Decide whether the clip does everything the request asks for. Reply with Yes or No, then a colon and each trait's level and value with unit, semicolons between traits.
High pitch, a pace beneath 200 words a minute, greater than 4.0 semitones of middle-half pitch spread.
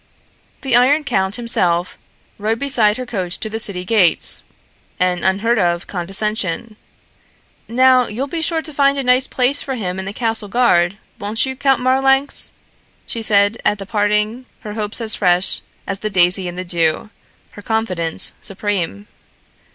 Yes: high, 215 Hz; average, 160 wpm; average, 5.0 semitones